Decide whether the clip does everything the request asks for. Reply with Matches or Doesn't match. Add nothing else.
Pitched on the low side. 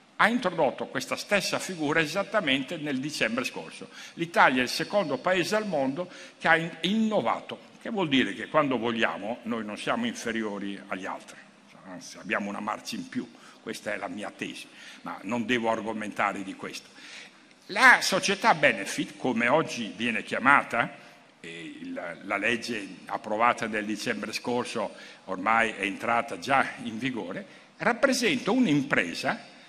Doesn't match